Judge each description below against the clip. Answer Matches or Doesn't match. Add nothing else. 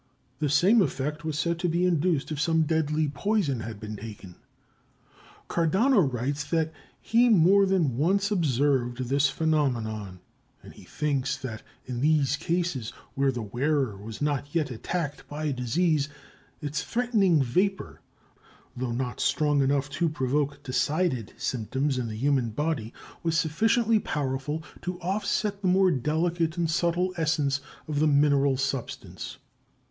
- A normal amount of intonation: Matches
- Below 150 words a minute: Matches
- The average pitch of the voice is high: Doesn't match